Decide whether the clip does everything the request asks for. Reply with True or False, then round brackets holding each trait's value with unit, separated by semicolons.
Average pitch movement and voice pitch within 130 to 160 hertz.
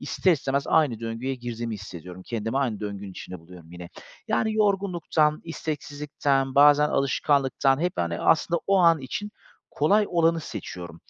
False (7.0 semitones; 135 Hz)